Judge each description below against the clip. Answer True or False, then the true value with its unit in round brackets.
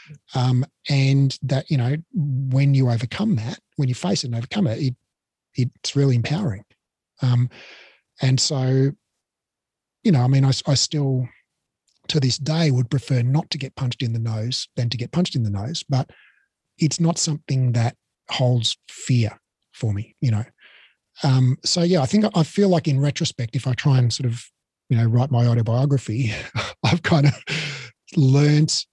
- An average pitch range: True (3.5 semitones)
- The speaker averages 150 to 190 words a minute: True (175 wpm)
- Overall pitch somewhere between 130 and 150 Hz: True (135 Hz)